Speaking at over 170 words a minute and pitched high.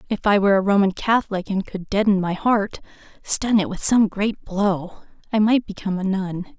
Yes: average, 200 wpm; high, 200 Hz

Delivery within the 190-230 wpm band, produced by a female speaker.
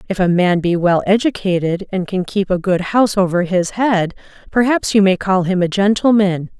Yes: average, 200 wpm; female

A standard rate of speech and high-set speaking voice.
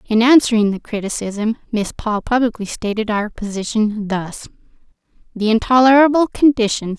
No: slow, 120 wpm; high, 225 Hz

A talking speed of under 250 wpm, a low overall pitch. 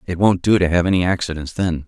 No: fast, 255 wpm; very low, 90 Hz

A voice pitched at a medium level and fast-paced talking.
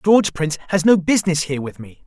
Yes: medium, 170 Hz; fast, 230 wpm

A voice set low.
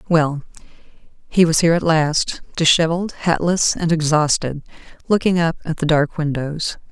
No: medium, 160 Hz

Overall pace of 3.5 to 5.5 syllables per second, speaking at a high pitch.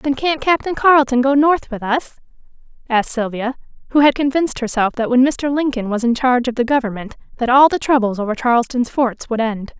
No: 5.8 syllables/s; very high, 255 Hz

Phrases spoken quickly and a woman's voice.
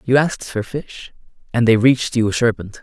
No: fast, 215 wpm; male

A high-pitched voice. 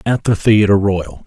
No: low, 100 Hz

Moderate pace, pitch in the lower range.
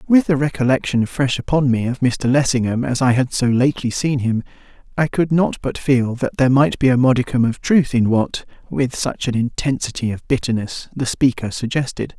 Yes: average, 195 wpm; low, 130 Hz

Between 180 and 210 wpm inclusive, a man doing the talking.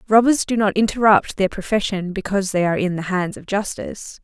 No: average, 200 wpm; female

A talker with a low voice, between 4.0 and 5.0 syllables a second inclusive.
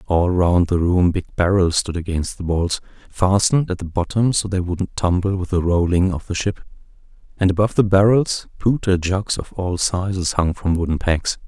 Yes: very low, 95 Hz; 4.9 syllables/s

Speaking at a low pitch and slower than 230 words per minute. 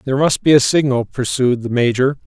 Yes: low, 130 Hz; fast, 205 wpm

